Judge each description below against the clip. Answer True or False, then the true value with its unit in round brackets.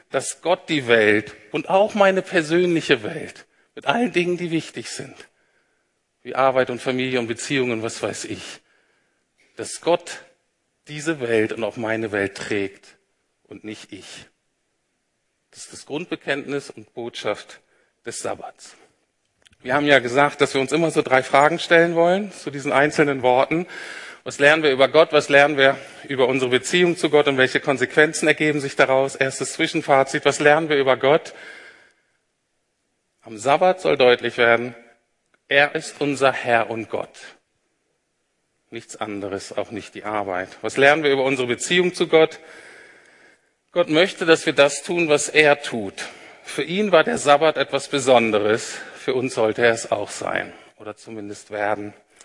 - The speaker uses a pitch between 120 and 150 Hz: True (140 Hz)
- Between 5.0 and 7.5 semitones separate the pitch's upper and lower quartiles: True (5.3 semitones)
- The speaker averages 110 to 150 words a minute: False (160 wpm)